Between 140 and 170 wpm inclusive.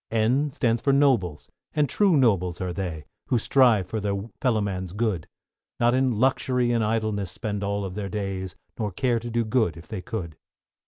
No: average, 180 wpm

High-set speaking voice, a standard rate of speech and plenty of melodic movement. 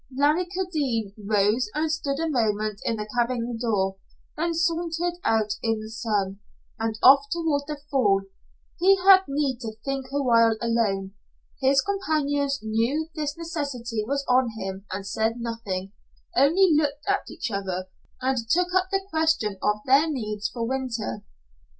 Yes: very high, 260 Hz; average, 155 wpm; wide, 6.2 semitones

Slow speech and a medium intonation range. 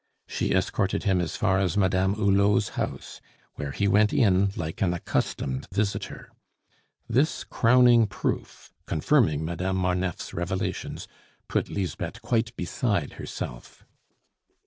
Yes: slow, 120 wpm; average, 3.3 semitones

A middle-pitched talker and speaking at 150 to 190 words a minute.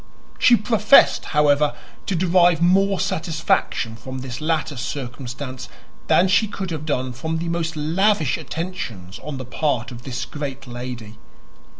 No: medium, 150 Hz; average, 140 wpm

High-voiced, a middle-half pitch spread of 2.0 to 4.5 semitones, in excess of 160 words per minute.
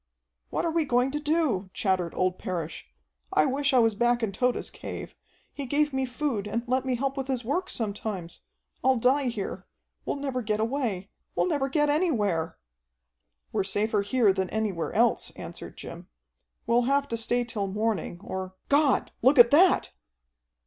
No: high, 240 Hz; average, 5.2 semitones; average, 170 wpm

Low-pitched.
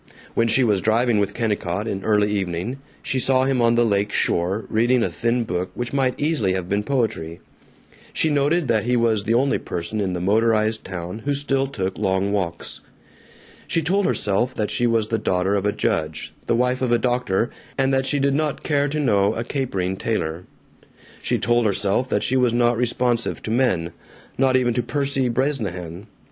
Yes: low, 115 Hz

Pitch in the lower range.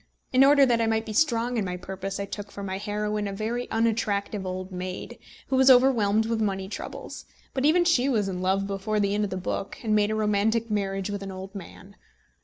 No: high, 210 Hz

